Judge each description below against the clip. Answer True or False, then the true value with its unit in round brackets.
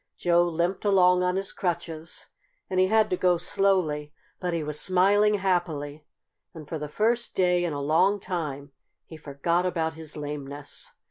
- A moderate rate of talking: True (170 wpm)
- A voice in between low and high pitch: True (175 Hz)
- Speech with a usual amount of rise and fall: True (3.6 semitones)